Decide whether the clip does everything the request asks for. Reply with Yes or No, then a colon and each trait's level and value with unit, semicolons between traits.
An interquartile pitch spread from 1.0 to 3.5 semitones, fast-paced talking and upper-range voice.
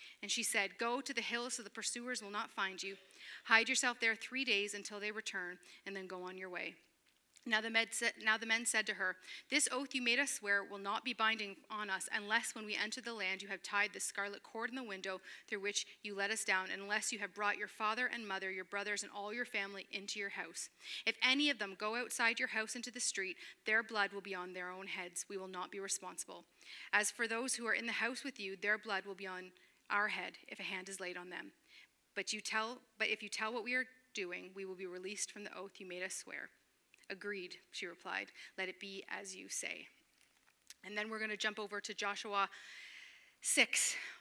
Yes: average, 2.7 semitones; fast, 240 wpm; high, 205 Hz